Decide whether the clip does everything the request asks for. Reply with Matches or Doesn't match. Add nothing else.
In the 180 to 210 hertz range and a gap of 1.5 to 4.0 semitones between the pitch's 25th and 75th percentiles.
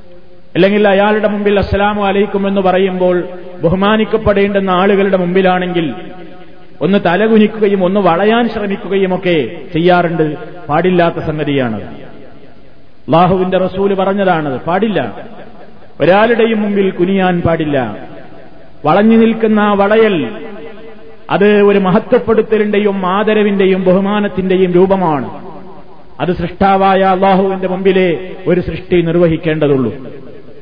Matches